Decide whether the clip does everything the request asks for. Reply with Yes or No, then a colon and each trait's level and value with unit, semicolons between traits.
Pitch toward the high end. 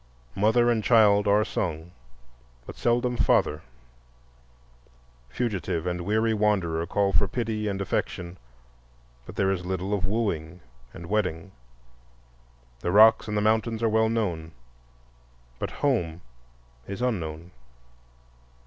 No: low, 100 Hz